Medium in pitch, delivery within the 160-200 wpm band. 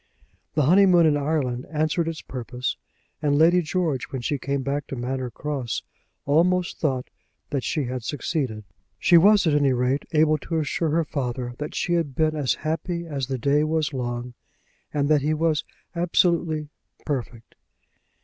Yes: medium, 150 Hz; average, 165 wpm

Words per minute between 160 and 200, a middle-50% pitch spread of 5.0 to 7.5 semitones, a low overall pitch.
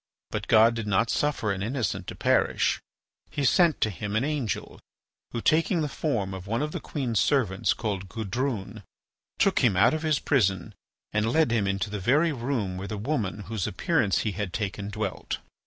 Yes: average, 190 wpm; wide, 5.6 semitones; low, 110 Hz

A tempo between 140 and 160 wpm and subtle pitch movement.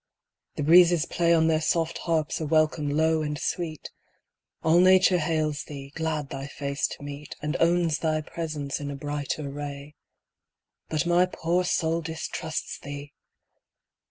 Yes: average, 150 wpm; narrow, 2.3 semitones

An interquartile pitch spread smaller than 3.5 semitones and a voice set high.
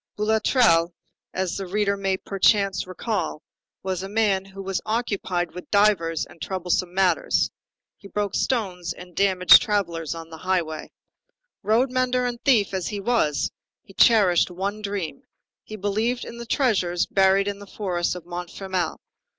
Yes: average, 2.9 semitones; high, 195 Hz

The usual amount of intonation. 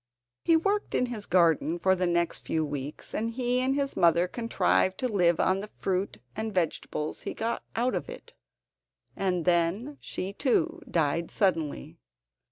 No: wide, 6.1 semitones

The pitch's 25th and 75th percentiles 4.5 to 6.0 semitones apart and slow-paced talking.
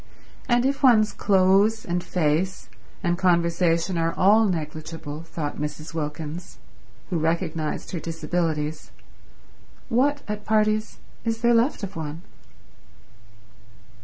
Yes: average, 4.8 semitones; slow, 110 wpm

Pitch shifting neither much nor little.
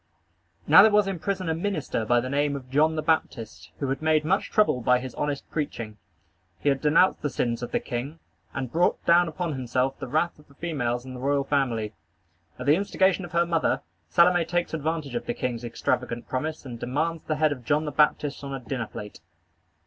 Yes: average, 4.5 semitones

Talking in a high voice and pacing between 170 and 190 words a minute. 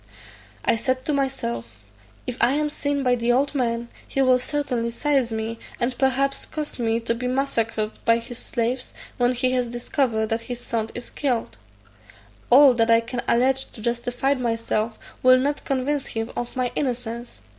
Yes: high, 245 Hz; average, 175 wpm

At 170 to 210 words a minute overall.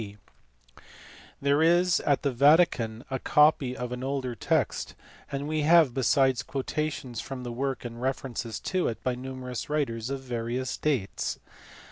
No: average, 150 wpm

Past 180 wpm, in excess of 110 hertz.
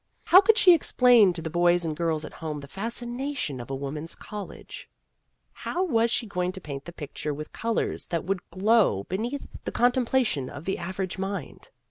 Yes: average, 195 wpm; medium, 185 Hz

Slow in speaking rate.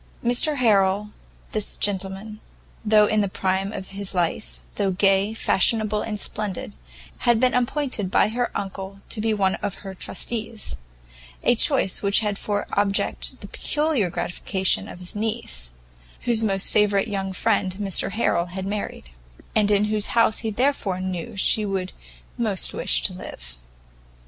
No: average, 155 wpm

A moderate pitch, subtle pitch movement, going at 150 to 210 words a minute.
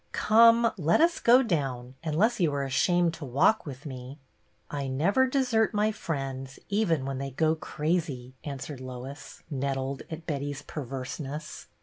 No: medium, 150 Hz; wide, 5.4 semitones; average, 155 wpm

